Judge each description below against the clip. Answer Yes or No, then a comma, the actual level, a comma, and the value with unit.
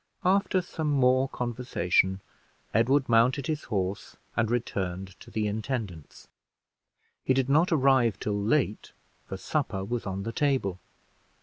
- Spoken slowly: Yes, slow, 130 wpm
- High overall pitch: No, low, 120 Hz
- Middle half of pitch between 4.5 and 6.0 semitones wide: Yes, average, 5.2 semitones